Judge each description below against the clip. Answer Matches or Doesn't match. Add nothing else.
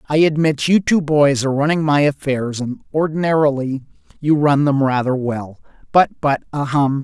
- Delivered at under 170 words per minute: Matches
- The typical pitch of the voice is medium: Matches